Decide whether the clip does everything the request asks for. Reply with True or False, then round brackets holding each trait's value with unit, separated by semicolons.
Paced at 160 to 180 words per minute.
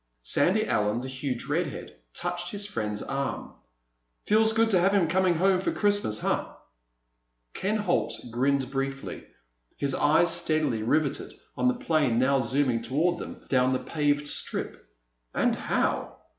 False (145 wpm)